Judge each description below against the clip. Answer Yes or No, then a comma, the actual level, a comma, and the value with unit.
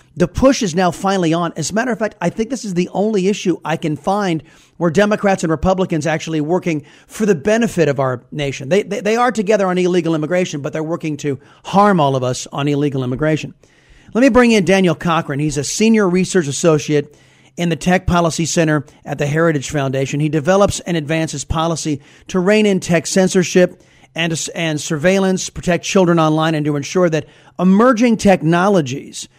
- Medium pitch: Yes, medium, 170 Hz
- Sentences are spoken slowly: No, average, 195 wpm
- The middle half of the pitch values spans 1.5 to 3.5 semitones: No, average, 3.9 semitones